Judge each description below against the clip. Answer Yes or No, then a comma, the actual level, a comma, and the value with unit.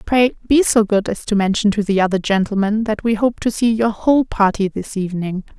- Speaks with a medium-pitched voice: No, high, 210 Hz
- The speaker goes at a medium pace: No, fast, 225 wpm